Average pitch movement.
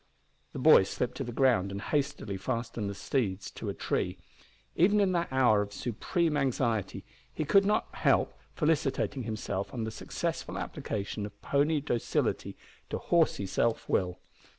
No: wide, 6.3 semitones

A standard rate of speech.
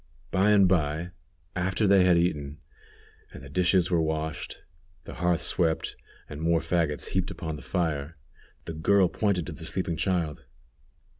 Yes: average, 155 wpm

